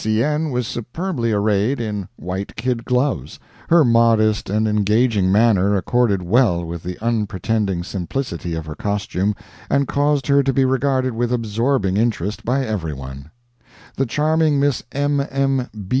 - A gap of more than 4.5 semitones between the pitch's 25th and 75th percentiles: Yes, average, 5.2 semitones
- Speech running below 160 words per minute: Yes, average, 150 wpm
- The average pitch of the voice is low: Yes, low, 115 Hz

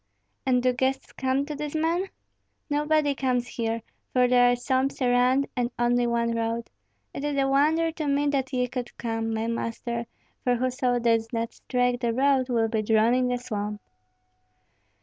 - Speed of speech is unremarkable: Yes, average, 180 wpm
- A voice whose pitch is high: Yes, very high, 250 Hz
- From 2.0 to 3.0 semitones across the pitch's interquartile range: Yes, average, 2.7 semitones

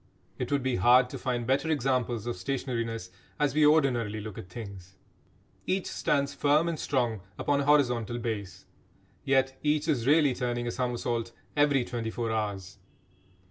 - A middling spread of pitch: Yes, average, 3.7 semitones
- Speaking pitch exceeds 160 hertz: No, low, 125 Hz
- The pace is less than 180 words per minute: Yes, average, 160 wpm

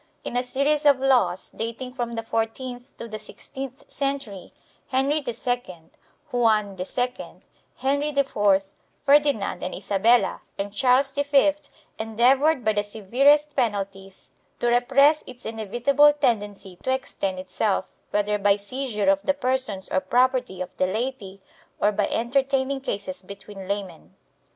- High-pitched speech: Yes, high, 235 Hz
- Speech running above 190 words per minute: No, slow, 135 wpm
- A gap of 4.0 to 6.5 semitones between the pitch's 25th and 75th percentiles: Yes, average, 4.9 semitones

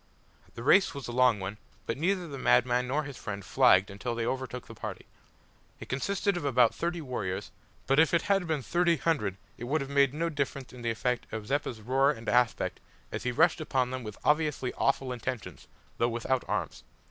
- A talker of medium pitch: No, low, 130 Hz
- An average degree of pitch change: Yes, average, 4.1 semitones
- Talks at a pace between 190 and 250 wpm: Yes, fast, 205 wpm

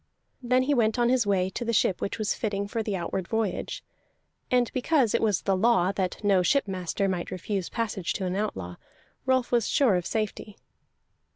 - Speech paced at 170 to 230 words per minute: Yes, average, 190 wpm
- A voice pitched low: No, high, 205 Hz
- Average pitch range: Yes, average, 4.0 semitones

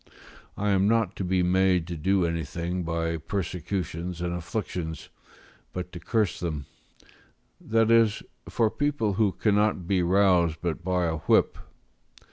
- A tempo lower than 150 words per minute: Yes, average, 140 wpm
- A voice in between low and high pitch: No, very low, 90 Hz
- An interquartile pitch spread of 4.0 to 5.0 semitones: No, average, 3.1 semitones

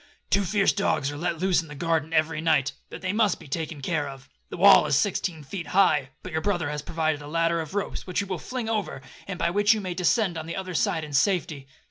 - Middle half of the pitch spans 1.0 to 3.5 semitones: No, average, 4.3 semitones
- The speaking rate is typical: No, fast, 240 wpm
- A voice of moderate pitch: Yes, medium, 165 Hz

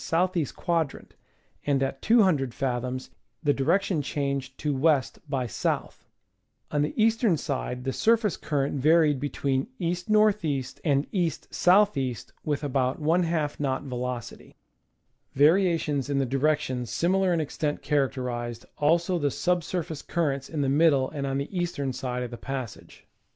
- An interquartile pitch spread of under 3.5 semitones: No, average, 3.9 semitones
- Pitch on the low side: No, medium, 145 Hz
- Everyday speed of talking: Yes, average, 155 wpm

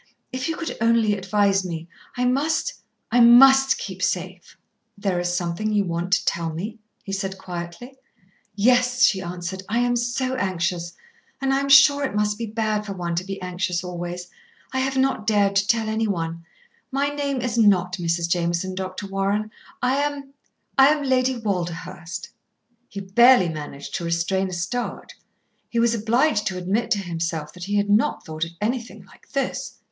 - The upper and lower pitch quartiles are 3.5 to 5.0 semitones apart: No, wide, 5.4 semitones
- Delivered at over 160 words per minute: Yes, average, 175 wpm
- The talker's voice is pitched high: Yes, high, 200 Hz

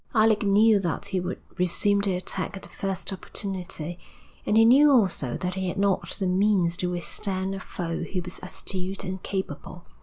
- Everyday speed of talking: Yes, average, 185 wpm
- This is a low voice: No, high, 190 Hz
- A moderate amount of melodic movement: No, narrow, 1.8 semitones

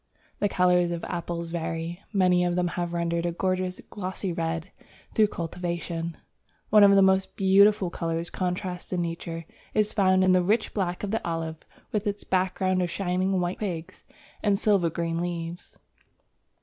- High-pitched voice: No, medium, 180 Hz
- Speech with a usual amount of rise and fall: No, narrow, 2.0 semitones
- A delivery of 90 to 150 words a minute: No, average, 165 wpm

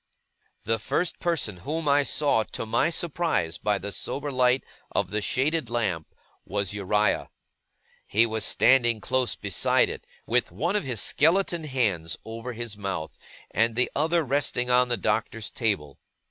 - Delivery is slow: No, average, 155 wpm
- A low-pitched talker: Yes, low, 120 Hz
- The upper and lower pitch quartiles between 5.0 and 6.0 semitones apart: Yes, average, 5.3 semitones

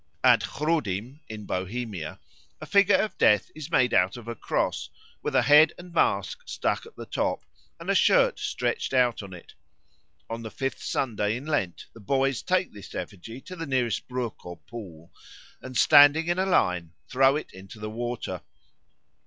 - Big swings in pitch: Yes, wide, 6.6 semitones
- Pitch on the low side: Yes, low, 125 Hz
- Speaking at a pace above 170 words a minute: Yes, average, 180 wpm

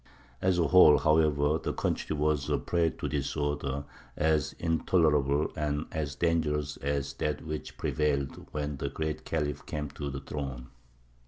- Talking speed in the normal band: Yes, average, 155 wpm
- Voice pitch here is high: No, very low, 75 Hz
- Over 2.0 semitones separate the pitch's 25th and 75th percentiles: No, narrow, 1.6 semitones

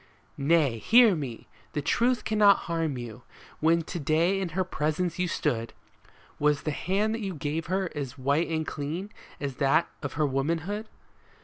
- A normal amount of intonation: Yes, average, 4.7 semitones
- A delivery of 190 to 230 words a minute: No, average, 170 wpm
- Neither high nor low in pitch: Yes, medium, 160 Hz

